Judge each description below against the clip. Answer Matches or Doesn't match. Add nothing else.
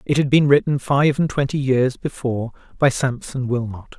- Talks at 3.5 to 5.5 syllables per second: Matches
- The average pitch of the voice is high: Doesn't match